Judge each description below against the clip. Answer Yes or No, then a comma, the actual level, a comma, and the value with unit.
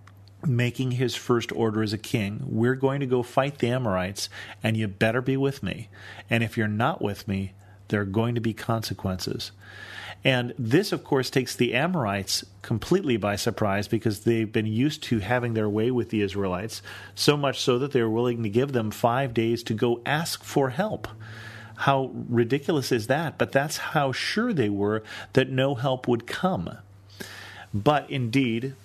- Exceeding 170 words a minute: Yes, average, 180 wpm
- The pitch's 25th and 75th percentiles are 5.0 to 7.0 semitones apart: No, average, 3.8 semitones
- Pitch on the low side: Yes, low, 115 Hz